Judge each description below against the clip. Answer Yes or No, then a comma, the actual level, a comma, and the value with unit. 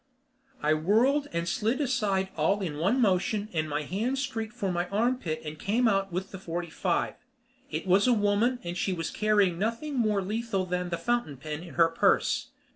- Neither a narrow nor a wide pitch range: Yes, average, 4.9 semitones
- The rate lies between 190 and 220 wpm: Yes, average, 195 wpm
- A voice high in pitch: Yes, high, 195 Hz